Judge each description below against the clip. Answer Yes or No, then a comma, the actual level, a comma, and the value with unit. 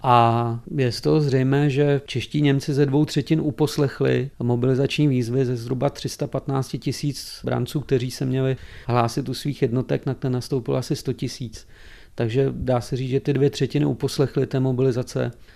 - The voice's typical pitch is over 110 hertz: Yes, low, 135 Hz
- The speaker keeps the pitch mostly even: Yes, narrow, 2.1 semitones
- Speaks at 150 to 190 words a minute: Yes, average, 165 wpm